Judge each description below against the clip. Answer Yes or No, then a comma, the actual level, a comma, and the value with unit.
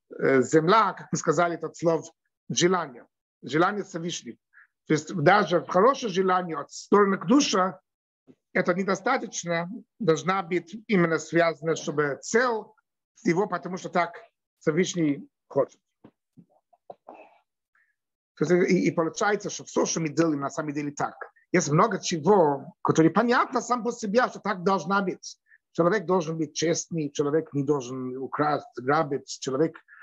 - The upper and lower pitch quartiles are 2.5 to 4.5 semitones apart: Yes, average, 4.0 semitones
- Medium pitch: Yes, medium, 175 Hz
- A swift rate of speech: No, average, 120 wpm